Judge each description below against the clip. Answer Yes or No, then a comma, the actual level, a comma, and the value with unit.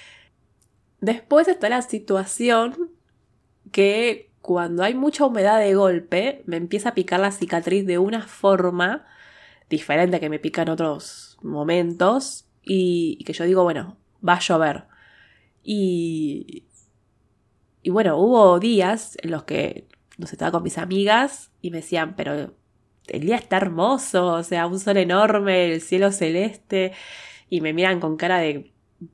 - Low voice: No, high, 190 Hz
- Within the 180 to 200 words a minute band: No, average, 150 wpm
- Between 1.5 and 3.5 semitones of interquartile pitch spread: No, average, 4.1 semitones